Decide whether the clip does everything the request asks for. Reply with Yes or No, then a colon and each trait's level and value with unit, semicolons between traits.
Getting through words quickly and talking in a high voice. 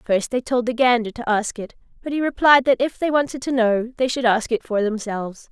Yes: fast, 250 wpm; high, 240 Hz